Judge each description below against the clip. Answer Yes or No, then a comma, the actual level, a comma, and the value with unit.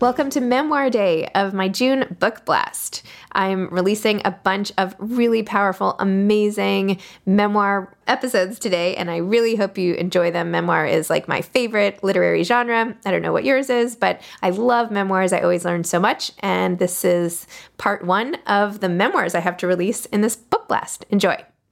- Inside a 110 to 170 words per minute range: No, average, 180 wpm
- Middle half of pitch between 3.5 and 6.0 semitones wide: Yes, average, 3.9 semitones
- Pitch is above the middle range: Yes, high, 195 Hz